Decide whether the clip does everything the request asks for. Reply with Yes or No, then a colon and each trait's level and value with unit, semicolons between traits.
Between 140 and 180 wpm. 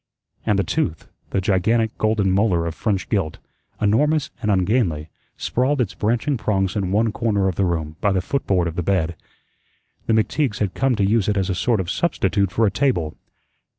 No: average, 190 wpm